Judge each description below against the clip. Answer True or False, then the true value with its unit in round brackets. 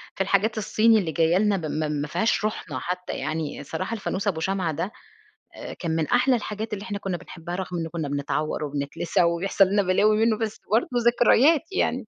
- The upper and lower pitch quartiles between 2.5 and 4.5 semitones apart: False (4.9 semitones)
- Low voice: False (185 Hz)